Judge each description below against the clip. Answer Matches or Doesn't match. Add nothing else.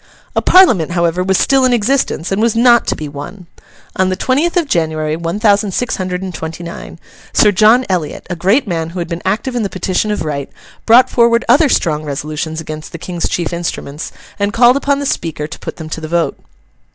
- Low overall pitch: Doesn't match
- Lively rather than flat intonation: Matches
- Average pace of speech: Doesn't match